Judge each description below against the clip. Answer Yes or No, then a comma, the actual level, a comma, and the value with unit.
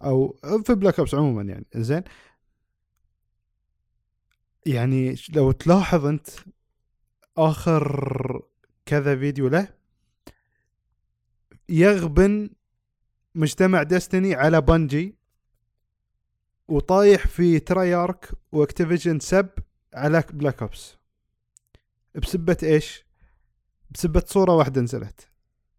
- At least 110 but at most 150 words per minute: No, average, 80 wpm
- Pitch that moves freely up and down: Yes, wide, 7.0 semitones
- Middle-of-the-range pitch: Yes, medium, 150 Hz